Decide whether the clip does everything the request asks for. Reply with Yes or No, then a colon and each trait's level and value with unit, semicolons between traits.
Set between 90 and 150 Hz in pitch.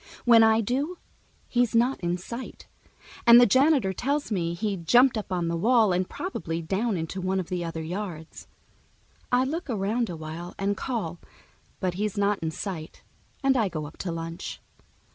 No: high, 195 Hz